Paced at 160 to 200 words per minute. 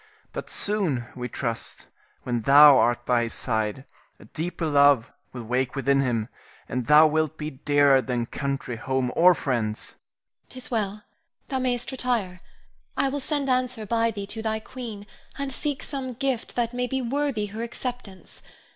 Yes: average, 165 wpm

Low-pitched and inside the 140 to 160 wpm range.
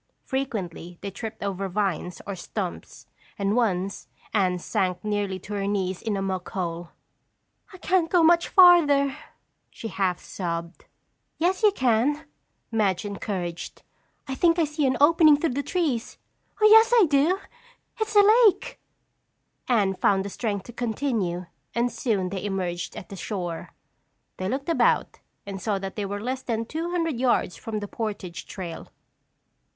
No: high, 215 Hz; average, 155 wpm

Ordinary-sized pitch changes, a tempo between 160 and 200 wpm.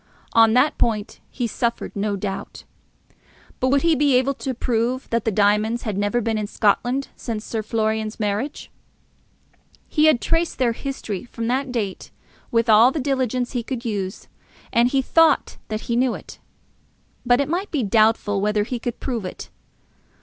Yes: average, 3.4 semitones; average, 170 wpm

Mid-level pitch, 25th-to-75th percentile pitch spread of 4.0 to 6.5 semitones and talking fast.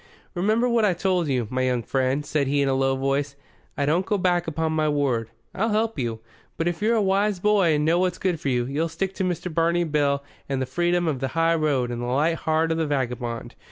Yes: medium, 155 Hz; average, 4.7 semitones; fast, 245 wpm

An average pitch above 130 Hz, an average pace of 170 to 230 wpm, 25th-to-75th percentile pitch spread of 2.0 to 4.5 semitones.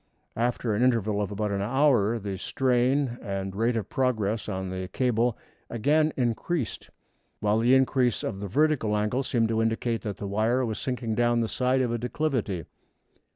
No: low, 115 Hz; average, 175 wpm; average, 3.3 semitones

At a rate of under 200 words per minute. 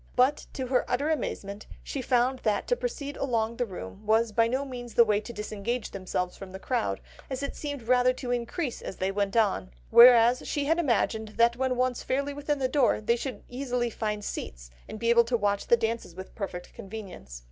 No: fast, 205 wpm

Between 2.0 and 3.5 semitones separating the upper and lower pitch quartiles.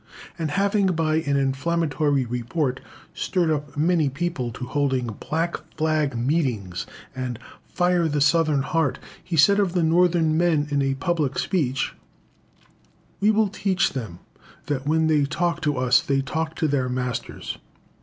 No: average, 4.0 semitones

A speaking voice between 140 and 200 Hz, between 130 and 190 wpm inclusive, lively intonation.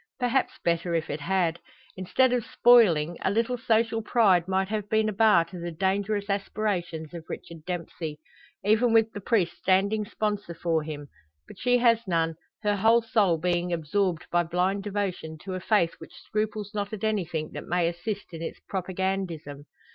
No: high, 190 Hz; average, 175 wpm; average, 4.1 semitones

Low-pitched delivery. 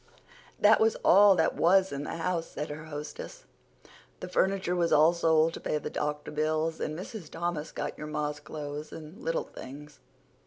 No: medium, 160 Hz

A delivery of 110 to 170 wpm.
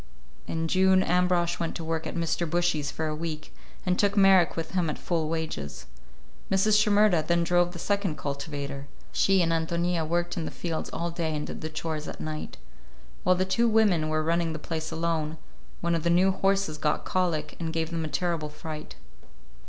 No: average, 195 wpm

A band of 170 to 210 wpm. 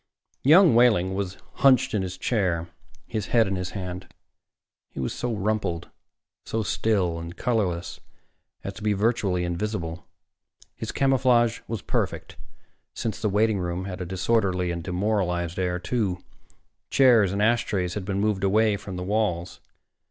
No: average, 150 wpm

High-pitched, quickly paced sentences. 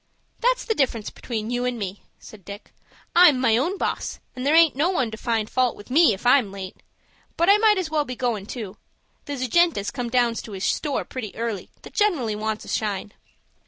Yes: high, 245 Hz; fast, 220 wpm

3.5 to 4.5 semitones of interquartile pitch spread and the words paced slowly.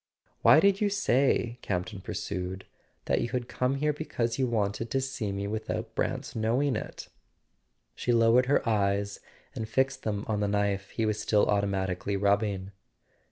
No: average, 3.9 semitones; average, 165 wpm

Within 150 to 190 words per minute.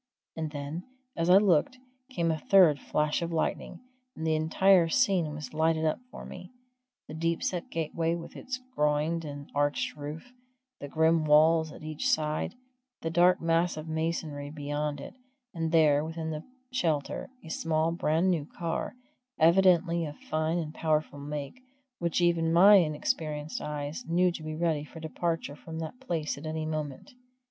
Yes: average, 165 wpm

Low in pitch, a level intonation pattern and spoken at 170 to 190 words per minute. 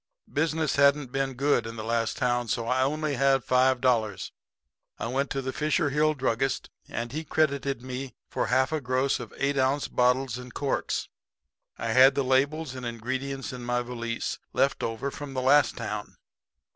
Yes: low, 130 Hz; narrow, 2.3 semitones; average, 180 wpm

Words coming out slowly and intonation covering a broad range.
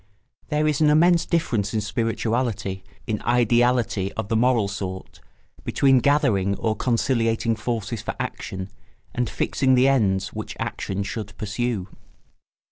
No: slow, 130 wpm; average, 4.0 semitones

